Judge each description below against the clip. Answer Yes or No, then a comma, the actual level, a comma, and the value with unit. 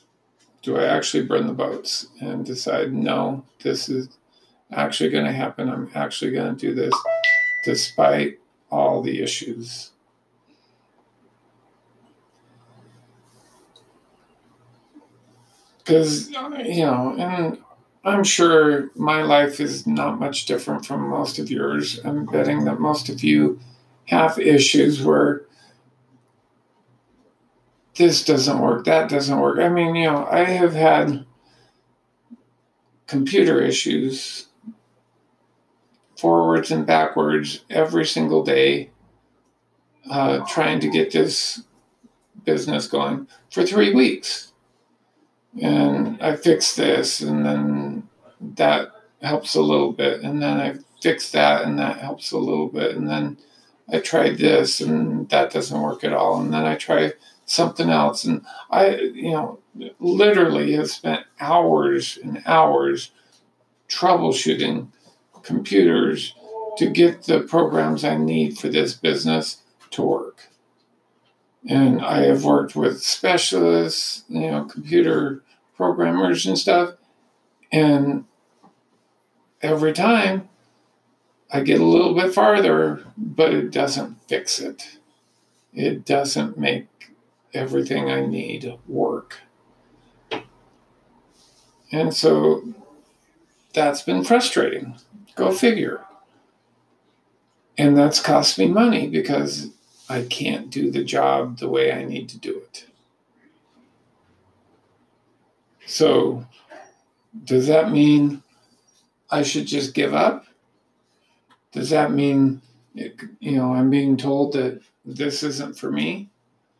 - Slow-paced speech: Yes, slow, 115 wpm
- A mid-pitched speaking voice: No, low, 125 Hz